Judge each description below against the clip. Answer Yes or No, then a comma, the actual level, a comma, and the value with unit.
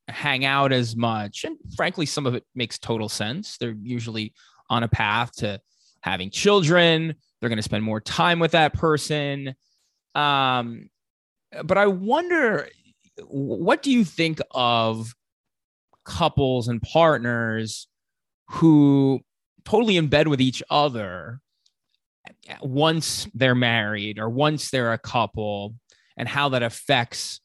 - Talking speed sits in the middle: No, slow, 130 wpm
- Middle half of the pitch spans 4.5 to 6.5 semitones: Yes, average, 5.2 semitones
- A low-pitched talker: Yes, low, 125 Hz